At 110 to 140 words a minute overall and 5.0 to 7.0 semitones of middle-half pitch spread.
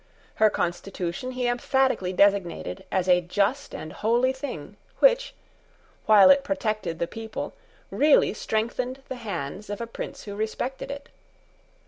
Yes: slow, 135 wpm; wide, 5.5 semitones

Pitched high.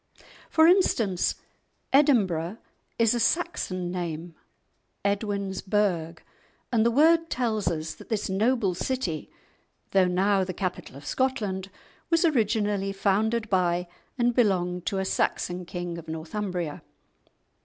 Yes: high, 195 Hz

